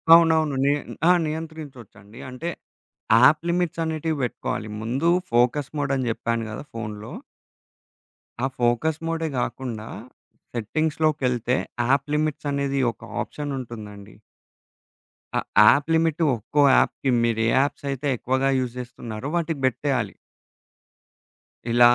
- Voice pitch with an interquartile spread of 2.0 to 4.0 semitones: No, average, 4.5 semitones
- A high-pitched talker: No, low, 135 Hz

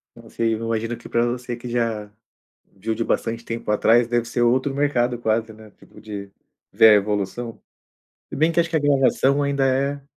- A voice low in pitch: Yes, low, 120 Hz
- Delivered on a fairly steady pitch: No, average, 3.1 semitones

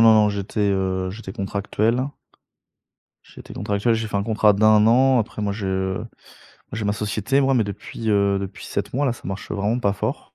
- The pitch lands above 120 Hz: No, low, 105 Hz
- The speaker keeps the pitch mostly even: Yes, narrow, 2.1 semitones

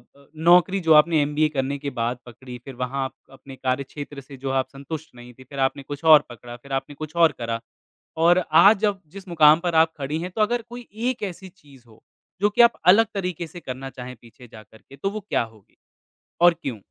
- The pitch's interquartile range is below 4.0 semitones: No, average, 5.0 semitones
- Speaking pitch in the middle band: Yes, medium, 145 Hz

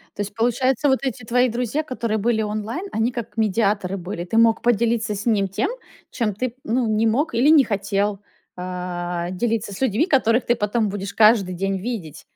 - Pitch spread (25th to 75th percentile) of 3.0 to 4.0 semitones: Yes, average, 3.3 semitones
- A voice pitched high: Yes, high, 220 Hz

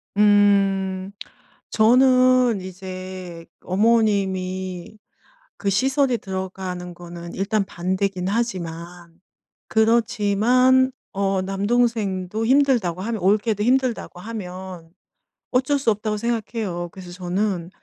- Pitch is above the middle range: Yes, high, 200 Hz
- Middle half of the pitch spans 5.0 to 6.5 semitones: No, average, 3.8 semitones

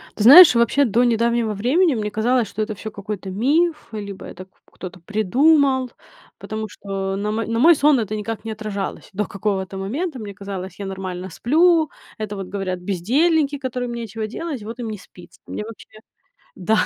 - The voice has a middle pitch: No, high, 220 Hz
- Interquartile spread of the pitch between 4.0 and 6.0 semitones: Yes, average, 4.4 semitones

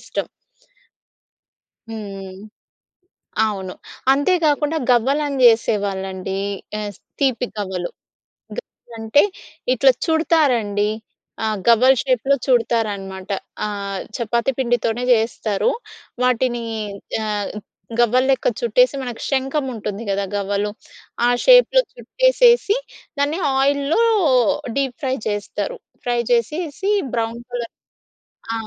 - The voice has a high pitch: Yes, high, 235 Hz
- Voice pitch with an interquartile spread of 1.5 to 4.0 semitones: No, average, 4.9 semitones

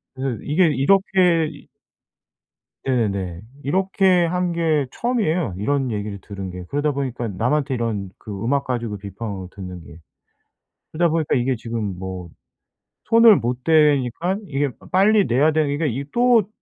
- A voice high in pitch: No, low, 135 Hz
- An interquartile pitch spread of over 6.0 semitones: Yes, wide, 7.8 semitones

